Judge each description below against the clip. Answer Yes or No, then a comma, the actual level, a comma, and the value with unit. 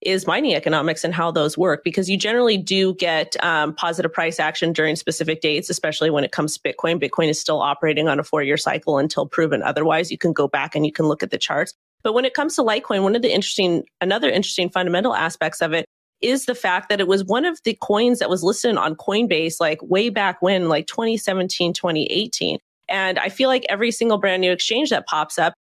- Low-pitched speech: No, medium, 180 Hz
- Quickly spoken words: Yes, fast, 225 wpm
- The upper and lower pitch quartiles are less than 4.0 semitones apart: No, average, 4.4 semitones